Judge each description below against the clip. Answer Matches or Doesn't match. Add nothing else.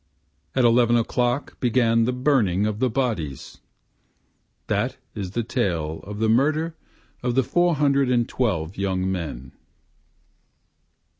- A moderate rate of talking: Doesn't match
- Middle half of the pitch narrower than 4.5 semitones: Doesn't match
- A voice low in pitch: Matches